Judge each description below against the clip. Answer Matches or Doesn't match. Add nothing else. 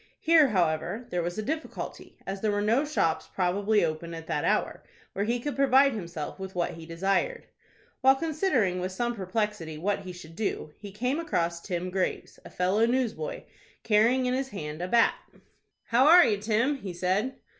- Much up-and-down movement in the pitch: Matches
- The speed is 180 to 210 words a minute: Matches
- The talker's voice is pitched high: Matches